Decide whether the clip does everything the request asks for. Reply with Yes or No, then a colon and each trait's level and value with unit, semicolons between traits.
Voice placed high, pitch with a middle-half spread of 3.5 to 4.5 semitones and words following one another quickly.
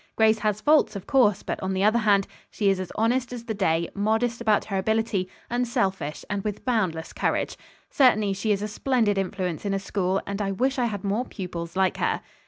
No: high, 205 Hz; average, 2.9 semitones; fast, 210 wpm